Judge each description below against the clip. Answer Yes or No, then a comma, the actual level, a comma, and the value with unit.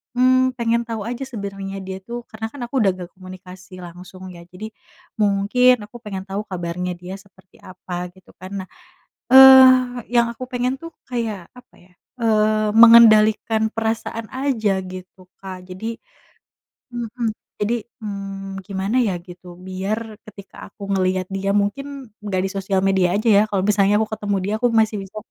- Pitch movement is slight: No, average, 3.6 semitones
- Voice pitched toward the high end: Yes, high, 205 Hz